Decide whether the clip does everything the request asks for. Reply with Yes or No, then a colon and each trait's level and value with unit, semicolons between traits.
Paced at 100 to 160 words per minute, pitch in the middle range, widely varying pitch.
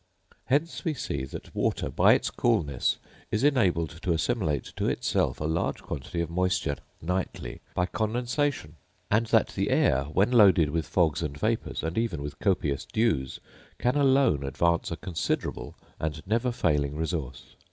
No: average, 155 wpm; very low, 85 Hz; wide, 7.4 semitones